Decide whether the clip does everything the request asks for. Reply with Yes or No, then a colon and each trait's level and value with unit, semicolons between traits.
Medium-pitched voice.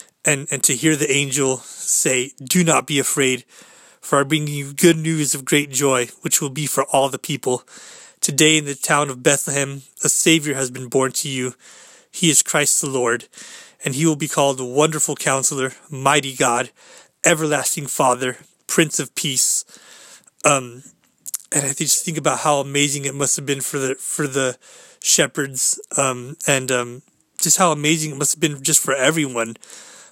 Yes: medium, 145 Hz